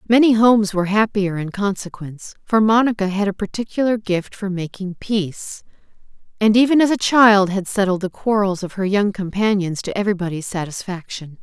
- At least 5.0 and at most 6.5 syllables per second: Yes, 5.5 syllables/s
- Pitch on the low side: No, high, 200 Hz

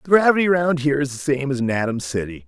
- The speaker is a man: Yes, male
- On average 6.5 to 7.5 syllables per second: Yes, 7.2 syllables/s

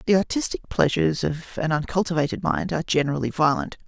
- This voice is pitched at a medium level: Yes, medium, 145 Hz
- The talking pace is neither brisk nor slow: Yes, average, 155 wpm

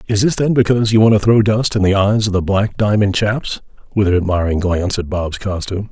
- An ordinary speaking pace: No, fast, 245 wpm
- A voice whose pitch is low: Yes, low, 100 Hz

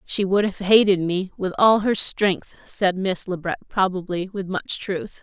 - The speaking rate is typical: Yes, average, 195 wpm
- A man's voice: No, female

